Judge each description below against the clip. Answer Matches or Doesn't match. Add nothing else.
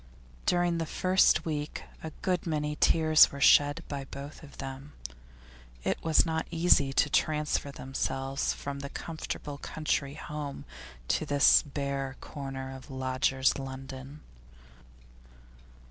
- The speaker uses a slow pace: Matches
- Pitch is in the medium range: Matches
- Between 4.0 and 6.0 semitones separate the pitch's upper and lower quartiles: Doesn't match